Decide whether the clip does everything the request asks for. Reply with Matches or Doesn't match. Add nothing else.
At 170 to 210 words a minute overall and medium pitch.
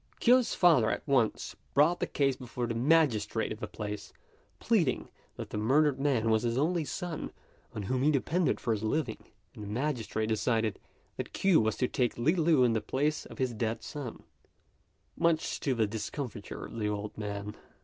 Doesn't match